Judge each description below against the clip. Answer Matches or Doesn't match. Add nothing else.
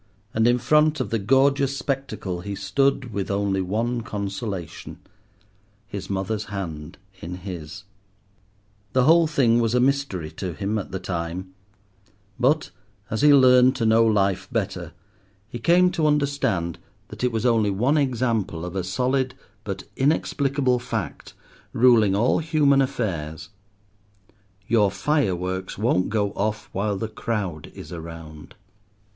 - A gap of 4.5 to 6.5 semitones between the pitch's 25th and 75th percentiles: Matches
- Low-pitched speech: Matches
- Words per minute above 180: Doesn't match